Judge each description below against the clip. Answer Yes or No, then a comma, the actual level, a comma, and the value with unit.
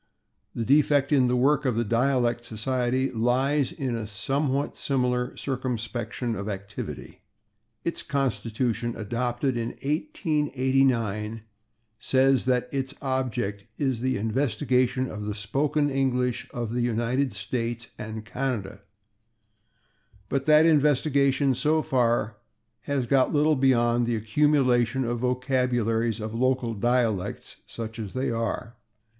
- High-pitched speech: No, low, 125 Hz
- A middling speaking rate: No, slow, 120 wpm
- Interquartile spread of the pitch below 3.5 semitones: Yes, average, 2.9 semitones